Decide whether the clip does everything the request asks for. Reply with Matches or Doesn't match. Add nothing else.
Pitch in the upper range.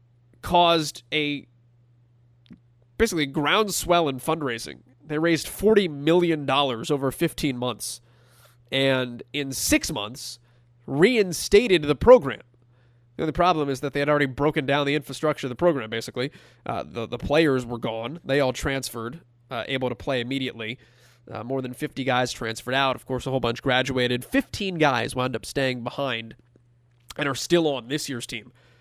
Doesn't match